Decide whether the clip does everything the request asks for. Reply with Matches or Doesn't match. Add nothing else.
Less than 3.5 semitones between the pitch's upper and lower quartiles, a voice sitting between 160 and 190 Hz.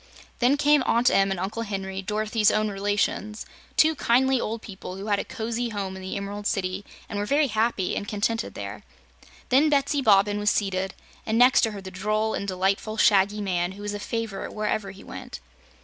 Doesn't match